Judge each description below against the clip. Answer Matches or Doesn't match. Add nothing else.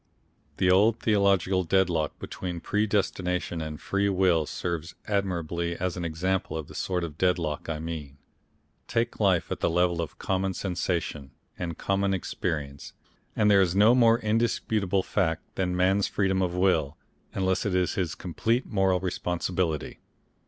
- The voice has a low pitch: Matches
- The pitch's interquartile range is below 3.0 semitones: Matches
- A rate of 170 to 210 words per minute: Doesn't match